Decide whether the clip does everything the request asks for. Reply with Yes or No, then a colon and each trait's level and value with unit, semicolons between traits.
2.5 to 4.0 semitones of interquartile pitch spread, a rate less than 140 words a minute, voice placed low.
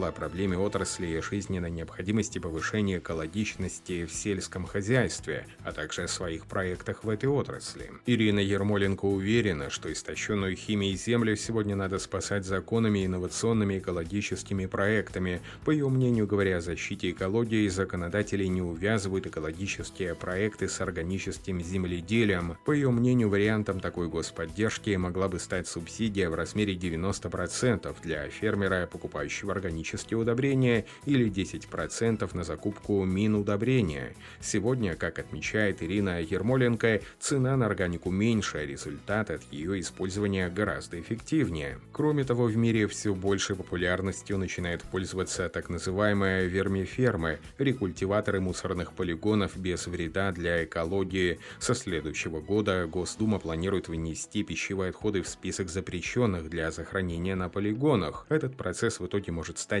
Yes: average, 3.1 semitones; average, 130 wpm; very low, 95 Hz